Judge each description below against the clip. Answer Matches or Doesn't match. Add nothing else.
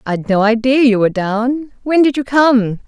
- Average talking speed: Doesn't match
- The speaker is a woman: Matches